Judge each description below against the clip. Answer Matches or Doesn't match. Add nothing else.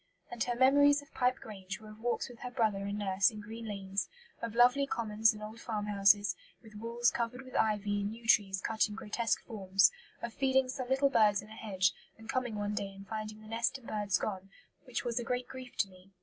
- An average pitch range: Matches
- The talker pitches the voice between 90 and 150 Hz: Doesn't match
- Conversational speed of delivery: Doesn't match